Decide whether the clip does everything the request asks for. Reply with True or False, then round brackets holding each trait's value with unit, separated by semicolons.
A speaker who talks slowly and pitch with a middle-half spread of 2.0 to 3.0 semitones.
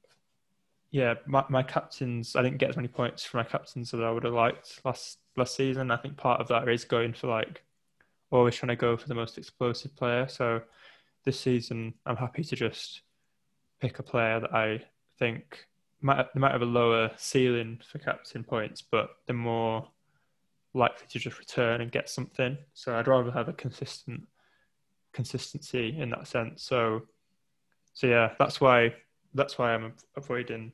False (180 wpm; 2.4 semitones)